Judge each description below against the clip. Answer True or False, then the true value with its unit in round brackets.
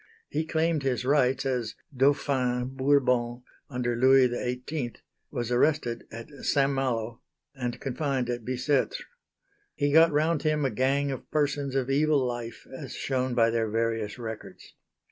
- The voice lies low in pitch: True (130 Hz)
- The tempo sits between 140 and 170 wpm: True (145 wpm)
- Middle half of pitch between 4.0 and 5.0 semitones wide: False (2.8 semitones)